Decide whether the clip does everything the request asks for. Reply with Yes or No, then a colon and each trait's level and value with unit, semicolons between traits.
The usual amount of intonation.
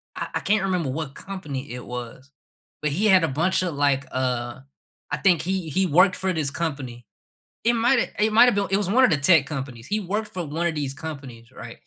No: wide, 5.9 semitones